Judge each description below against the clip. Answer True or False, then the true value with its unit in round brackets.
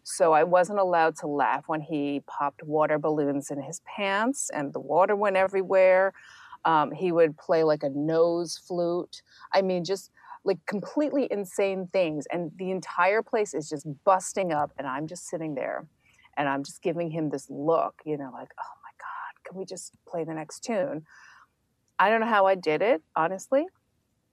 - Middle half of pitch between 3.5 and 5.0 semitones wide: True (4.0 semitones)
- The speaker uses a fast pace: False (185 wpm)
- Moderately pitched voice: True (175 Hz)